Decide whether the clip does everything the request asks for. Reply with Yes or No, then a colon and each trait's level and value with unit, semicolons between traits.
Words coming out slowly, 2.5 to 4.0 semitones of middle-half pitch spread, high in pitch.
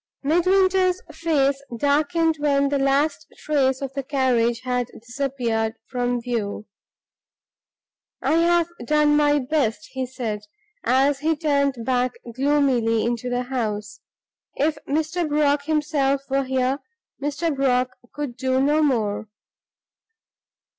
Yes: slow, 120 wpm; average, 3.2 semitones; very high, 275 Hz